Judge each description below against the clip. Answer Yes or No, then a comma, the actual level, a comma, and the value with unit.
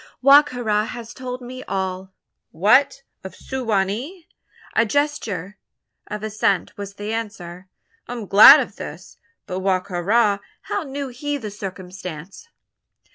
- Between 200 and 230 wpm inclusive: No, average, 150 wpm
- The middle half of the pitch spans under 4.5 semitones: No, average, 4.9 semitones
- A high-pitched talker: Yes, high, 210 Hz